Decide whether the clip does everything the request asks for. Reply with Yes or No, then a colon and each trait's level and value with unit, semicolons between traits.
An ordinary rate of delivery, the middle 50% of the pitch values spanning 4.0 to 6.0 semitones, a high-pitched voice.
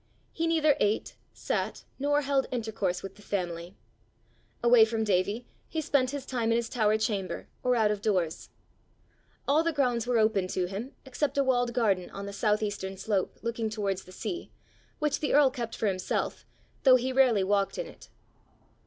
Yes: average, 180 wpm; average, 4.6 semitones; high, 225 Hz